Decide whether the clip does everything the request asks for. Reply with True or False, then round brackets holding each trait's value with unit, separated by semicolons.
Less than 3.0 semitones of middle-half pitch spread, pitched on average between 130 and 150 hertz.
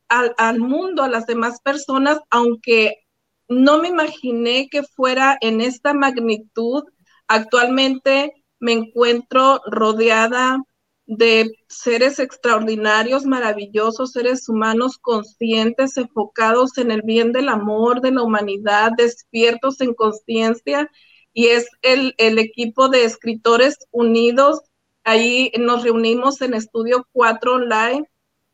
False (2.5 semitones; 235 Hz)